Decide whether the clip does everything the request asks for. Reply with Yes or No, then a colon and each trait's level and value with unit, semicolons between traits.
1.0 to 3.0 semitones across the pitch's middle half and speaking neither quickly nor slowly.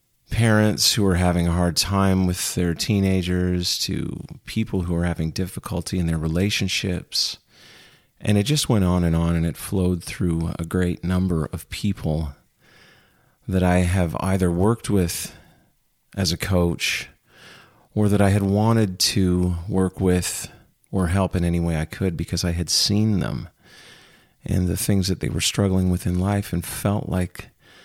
Yes: narrow, 2.4 semitones; average, 165 wpm